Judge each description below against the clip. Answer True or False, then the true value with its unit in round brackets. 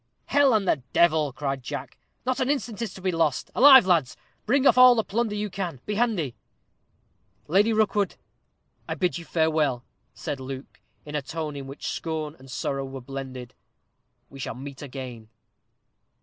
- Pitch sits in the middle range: True (160 Hz)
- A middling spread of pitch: False (7.4 semitones)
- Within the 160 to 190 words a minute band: True (170 wpm)